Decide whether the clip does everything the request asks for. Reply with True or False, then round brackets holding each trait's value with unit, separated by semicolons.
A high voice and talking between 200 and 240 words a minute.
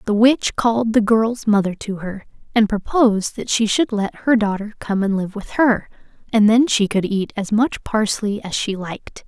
True (215 Hz; 205 wpm)